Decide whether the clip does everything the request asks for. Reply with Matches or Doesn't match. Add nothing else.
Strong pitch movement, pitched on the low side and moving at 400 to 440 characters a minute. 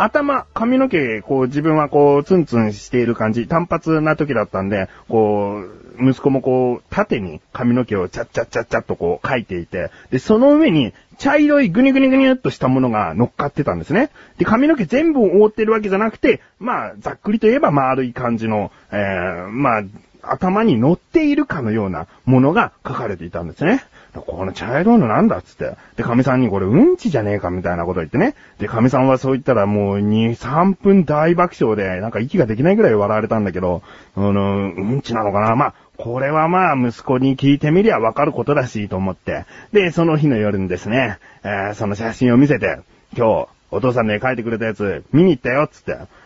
Matches